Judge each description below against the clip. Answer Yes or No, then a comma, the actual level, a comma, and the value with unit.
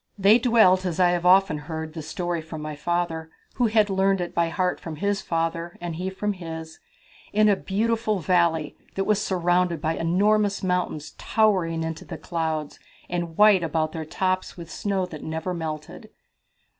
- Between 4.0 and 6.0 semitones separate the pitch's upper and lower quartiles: No, average, 3.1 semitones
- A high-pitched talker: No, medium, 175 Hz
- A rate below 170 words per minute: No, average, 175 wpm